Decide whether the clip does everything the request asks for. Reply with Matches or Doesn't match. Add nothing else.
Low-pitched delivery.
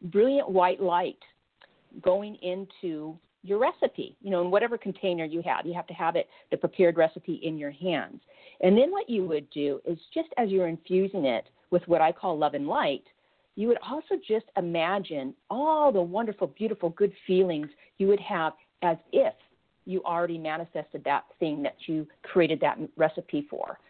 Doesn't match